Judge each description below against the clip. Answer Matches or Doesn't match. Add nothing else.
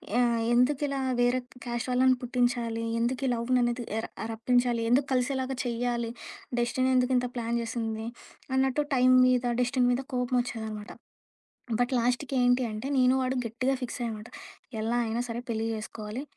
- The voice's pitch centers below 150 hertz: Doesn't match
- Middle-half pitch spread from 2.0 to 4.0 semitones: Doesn't match